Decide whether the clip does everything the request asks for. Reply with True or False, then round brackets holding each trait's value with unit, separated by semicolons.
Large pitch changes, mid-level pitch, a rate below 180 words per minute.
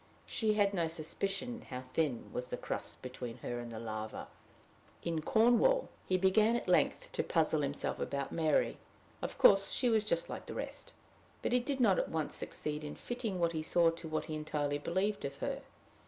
False (6.5 semitones; 165 Hz; 195 wpm)